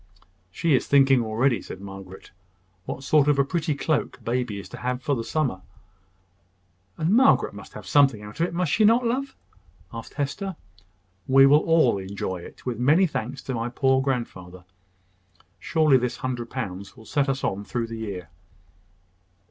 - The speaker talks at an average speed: Yes, average, 170 wpm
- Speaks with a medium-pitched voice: No, low, 130 Hz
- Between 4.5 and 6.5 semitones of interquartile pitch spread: Yes, average, 5.0 semitones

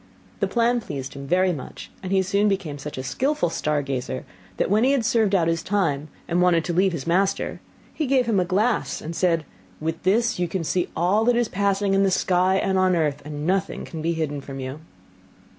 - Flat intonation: No, average, 4.4 semitones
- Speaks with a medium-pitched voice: Yes, medium, 180 Hz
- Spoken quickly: Yes, fast, 220 wpm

